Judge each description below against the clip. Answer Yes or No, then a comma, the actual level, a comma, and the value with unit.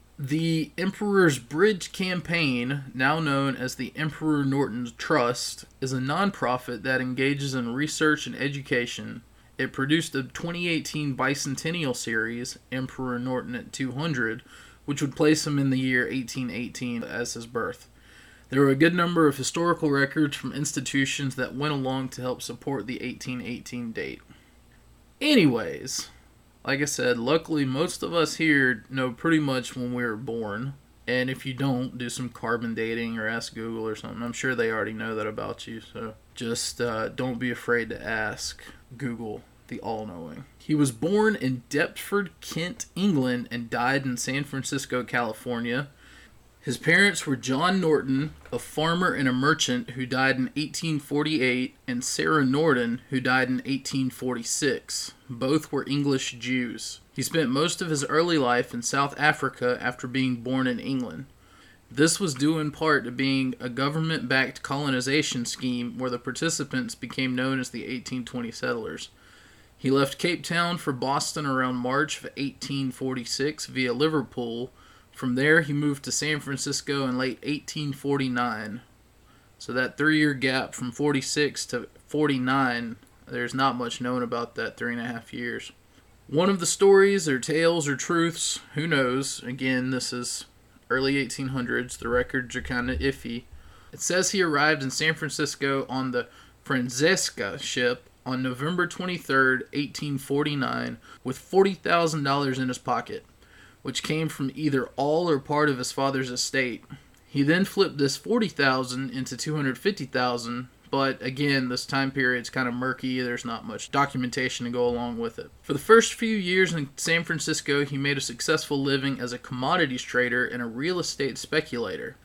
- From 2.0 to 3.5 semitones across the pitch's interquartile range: Yes, average, 3.1 semitones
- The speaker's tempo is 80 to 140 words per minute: No, average, 160 wpm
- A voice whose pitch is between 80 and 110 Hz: No, low, 135 Hz